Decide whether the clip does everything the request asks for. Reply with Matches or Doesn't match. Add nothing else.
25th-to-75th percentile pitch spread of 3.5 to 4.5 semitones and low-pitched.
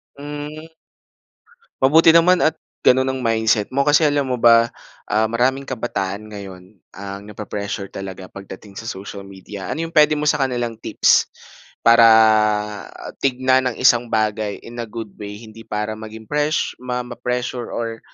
Matches